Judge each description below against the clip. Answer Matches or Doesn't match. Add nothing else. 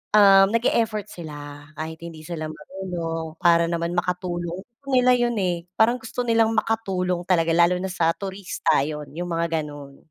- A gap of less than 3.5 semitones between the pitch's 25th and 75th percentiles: Doesn't match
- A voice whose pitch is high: Doesn't match